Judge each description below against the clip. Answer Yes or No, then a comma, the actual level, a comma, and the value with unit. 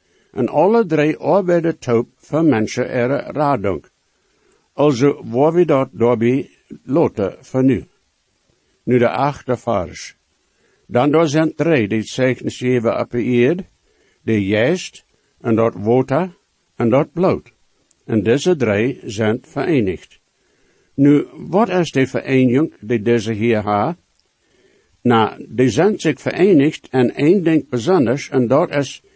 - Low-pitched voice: Yes, low, 130 Hz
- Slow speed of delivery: Yes, slow, 130 wpm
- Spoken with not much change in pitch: No, average, 4.8 semitones